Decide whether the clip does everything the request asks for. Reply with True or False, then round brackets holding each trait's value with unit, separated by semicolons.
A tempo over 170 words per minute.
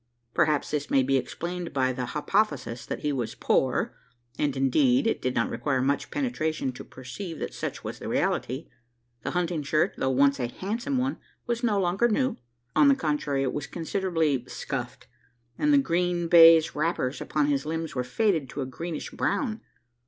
True (180 wpm)